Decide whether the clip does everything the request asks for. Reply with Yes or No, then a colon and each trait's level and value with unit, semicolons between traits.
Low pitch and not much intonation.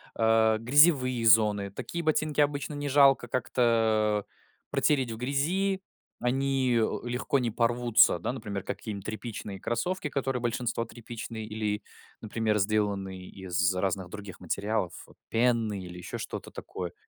No: low, 115 Hz; average, 3.8 semitones